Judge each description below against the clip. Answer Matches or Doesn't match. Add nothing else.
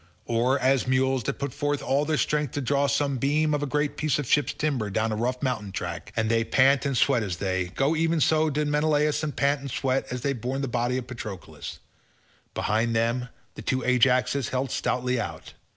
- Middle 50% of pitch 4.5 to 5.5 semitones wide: Doesn't match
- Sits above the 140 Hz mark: Doesn't match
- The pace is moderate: Doesn't match